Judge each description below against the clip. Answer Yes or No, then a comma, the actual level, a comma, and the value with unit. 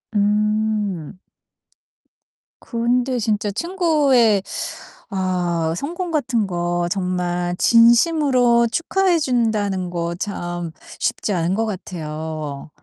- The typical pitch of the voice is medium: No, high, 210 Hz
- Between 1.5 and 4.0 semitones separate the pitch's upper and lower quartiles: No, wide, 5.6 semitones